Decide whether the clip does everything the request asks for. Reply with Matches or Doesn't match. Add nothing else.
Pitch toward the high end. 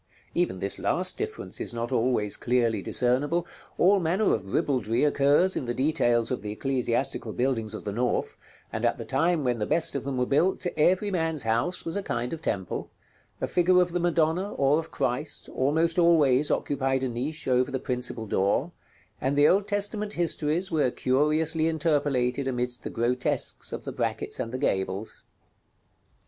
Doesn't match